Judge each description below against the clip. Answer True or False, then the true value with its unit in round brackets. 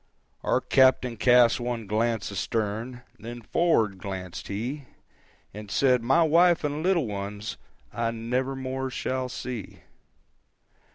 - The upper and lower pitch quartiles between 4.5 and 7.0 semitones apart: False (3.7 semitones)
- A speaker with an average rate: False (120 wpm)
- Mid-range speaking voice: False (120 Hz)